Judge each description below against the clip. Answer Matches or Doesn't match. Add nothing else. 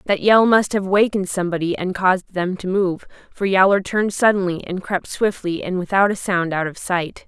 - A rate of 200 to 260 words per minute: Matches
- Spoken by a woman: Matches